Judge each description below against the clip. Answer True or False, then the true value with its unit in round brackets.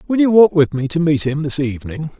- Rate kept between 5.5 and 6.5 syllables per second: True (6.0 syllables/s)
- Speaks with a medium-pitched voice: True (155 Hz)